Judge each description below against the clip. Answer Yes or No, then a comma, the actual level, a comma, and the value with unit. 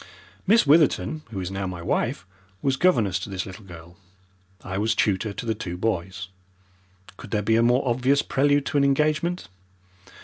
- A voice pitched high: No, low, 110 Hz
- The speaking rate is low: No, average, 175 wpm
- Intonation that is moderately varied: No, wide, 6.8 semitones